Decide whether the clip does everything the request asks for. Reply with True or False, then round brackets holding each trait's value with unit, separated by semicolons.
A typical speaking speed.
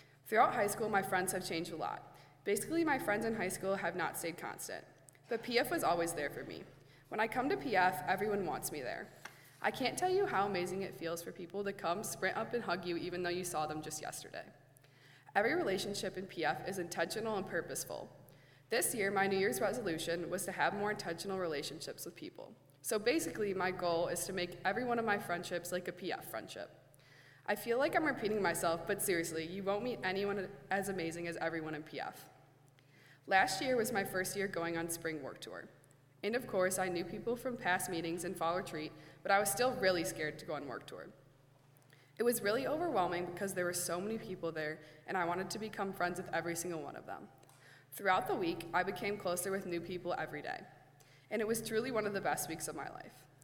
False (220 wpm)